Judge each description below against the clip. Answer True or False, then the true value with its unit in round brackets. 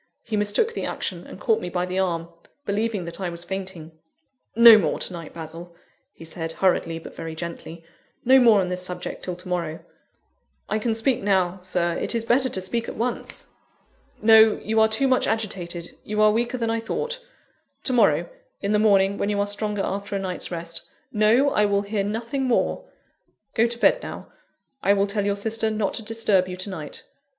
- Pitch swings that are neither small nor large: True (3.9 semitones)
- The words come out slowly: False (200 wpm)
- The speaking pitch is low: False (200 Hz)